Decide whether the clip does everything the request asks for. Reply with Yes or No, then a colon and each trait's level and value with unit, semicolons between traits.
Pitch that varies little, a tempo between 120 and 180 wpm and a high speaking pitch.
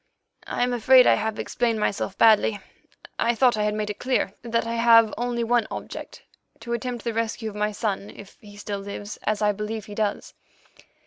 No: narrow, 2.1 semitones; average, 195 wpm; high, 220 Hz